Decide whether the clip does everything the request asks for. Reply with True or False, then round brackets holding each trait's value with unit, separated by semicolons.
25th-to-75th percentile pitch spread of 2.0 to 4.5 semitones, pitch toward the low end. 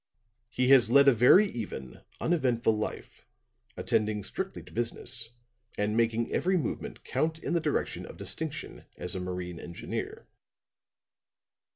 False (5.0 semitones; 115 Hz)